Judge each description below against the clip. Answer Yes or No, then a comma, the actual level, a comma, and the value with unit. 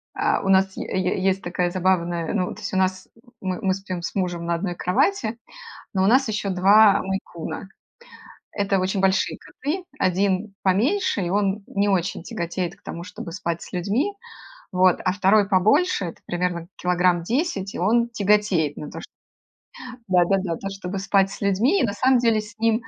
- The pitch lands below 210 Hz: Yes, high, 190 Hz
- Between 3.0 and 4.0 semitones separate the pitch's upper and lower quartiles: No, narrow, 2.4 semitones